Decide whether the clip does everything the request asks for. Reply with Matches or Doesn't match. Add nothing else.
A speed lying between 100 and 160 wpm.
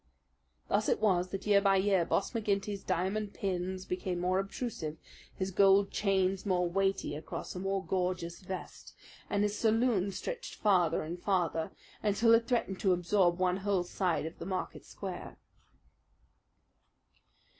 Matches